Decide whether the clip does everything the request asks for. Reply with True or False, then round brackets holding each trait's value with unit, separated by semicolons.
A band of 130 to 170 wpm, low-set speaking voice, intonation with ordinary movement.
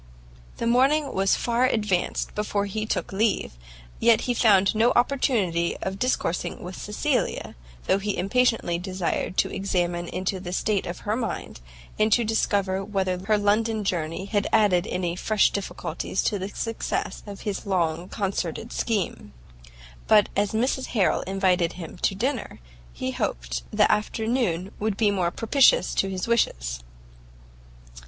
False (145 wpm; 200 Hz; 3.5 semitones)